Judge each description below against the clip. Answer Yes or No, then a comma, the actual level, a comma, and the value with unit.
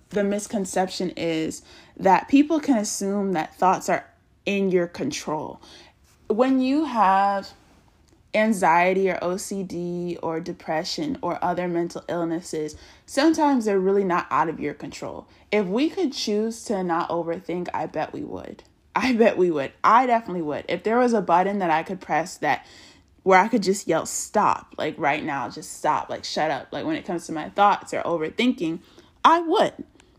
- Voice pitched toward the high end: Yes, high, 195 Hz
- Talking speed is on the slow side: No, average, 170 wpm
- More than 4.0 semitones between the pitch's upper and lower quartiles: Yes, average, 5.1 semitones